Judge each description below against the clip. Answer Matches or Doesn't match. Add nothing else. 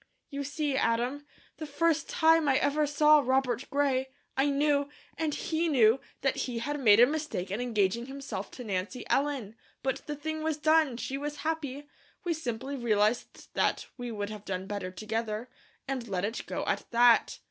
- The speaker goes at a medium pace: Matches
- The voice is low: Doesn't match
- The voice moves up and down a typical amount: Matches